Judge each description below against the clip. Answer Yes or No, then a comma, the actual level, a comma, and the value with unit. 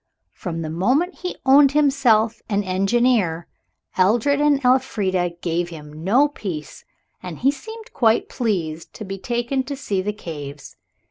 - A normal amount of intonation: No, wide, 7.3 semitones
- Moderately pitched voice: No, high, 215 Hz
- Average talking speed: Yes, average, 145 wpm